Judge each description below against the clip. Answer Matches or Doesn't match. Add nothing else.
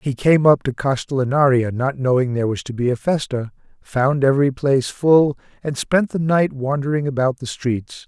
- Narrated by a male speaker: Matches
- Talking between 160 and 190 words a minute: Matches